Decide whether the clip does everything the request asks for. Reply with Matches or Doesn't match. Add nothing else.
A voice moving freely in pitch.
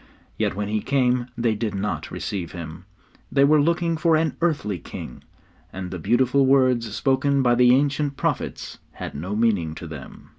Matches